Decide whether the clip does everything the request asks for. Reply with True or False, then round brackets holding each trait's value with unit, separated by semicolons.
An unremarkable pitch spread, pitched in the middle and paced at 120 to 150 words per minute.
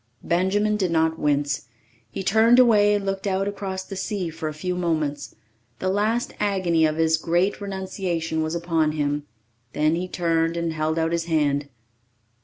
False (3.4 semitones; 170 Hz; 170 wpm)